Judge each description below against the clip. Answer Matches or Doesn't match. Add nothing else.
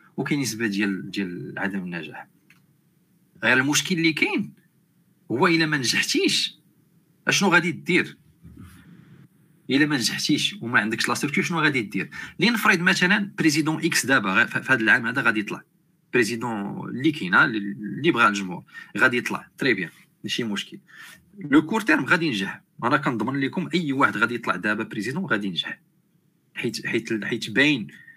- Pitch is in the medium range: Matches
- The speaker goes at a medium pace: Doesn't match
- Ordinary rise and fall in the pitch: Doesn't match